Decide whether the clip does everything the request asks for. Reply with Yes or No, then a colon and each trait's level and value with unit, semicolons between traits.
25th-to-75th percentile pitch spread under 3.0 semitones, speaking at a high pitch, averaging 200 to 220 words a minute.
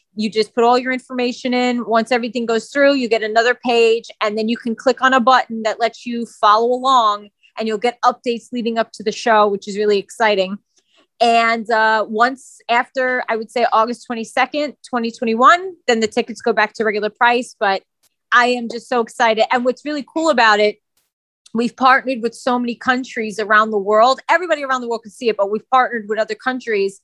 Yes: narrow, 2.5 semitones; high, 235 Hz; fast, 205 wpm